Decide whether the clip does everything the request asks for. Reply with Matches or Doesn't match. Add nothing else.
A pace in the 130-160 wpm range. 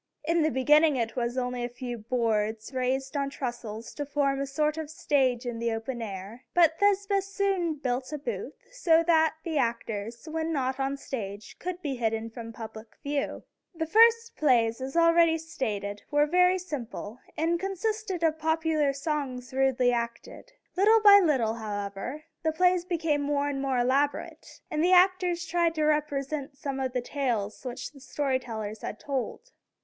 Doesn't match